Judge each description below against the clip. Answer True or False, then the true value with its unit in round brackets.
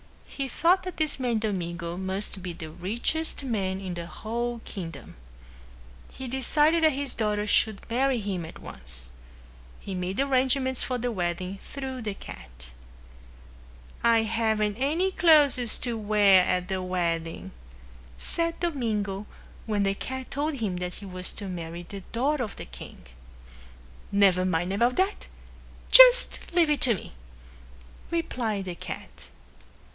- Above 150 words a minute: False (145 wpm)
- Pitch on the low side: False (215 Hz)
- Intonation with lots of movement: True (6.3 semitones)